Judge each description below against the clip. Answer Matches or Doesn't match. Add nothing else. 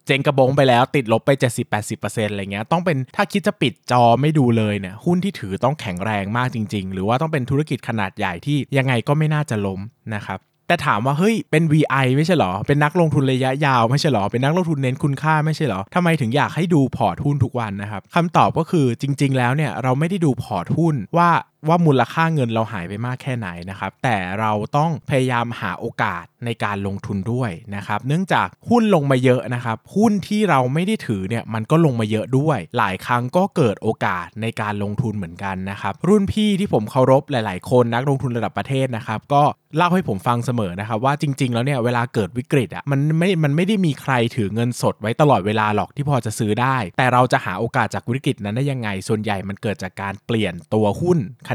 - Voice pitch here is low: Matches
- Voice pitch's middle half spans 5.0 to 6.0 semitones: Matches